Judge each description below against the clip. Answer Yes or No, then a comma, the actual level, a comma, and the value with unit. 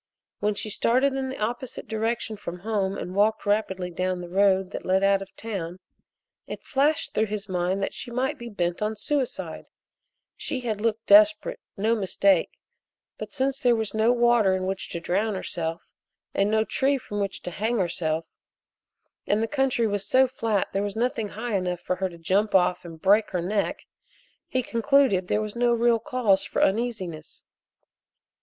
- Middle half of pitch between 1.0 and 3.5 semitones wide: No, average, 3.9 semitones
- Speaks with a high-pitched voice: Yes, high, 210 Hz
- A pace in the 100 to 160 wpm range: No, average, 185 wpm